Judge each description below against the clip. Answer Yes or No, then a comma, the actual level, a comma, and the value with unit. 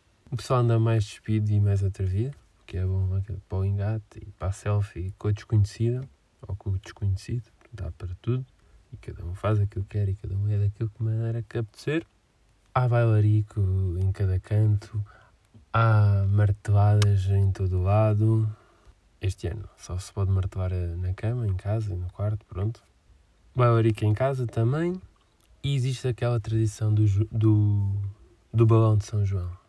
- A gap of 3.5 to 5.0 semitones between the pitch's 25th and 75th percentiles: No, narrow, 2.6 semitones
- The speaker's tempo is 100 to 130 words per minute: No, average, 170 wpm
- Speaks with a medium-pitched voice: No, low, 105 Hz